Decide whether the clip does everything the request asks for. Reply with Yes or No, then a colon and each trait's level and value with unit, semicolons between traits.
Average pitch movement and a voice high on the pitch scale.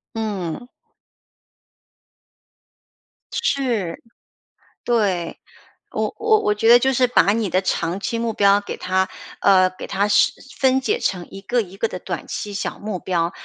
Yes: average, 4.2 semitones; high, 205 Hz